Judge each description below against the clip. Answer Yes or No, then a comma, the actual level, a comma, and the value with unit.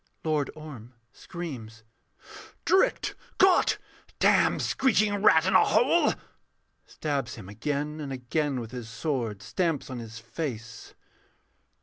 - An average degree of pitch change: No, wide, 6.0 semitones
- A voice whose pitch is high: No, medium, 145 Hz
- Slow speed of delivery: Yes, slow, 115 wpm